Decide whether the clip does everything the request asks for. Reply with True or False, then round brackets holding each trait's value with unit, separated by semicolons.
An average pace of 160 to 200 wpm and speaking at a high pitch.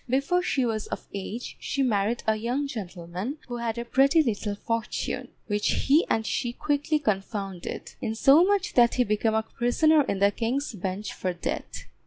True (170 wpm; 235 Hz)